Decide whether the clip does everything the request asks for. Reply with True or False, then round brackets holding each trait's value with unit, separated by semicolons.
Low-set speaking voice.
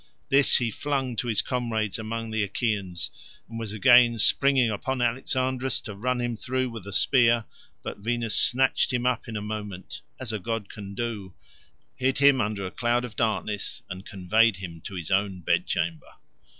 True (115 Hz)